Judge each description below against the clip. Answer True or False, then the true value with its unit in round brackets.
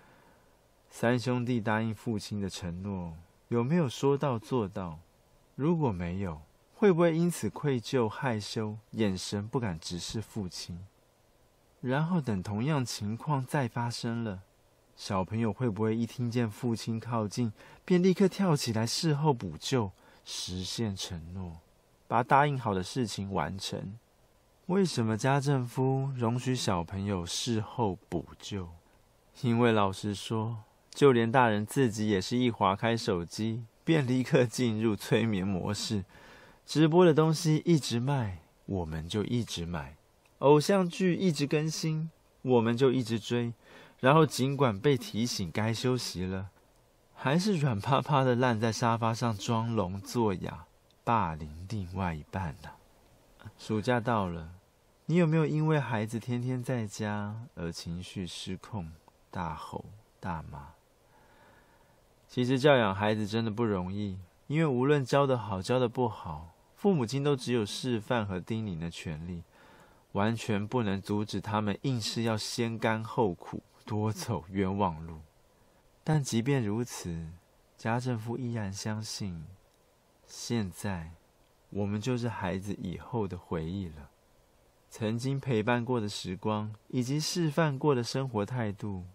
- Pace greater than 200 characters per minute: True (210 characters per minute)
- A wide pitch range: False (4.6 semitones)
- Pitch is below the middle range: True (115 Hz)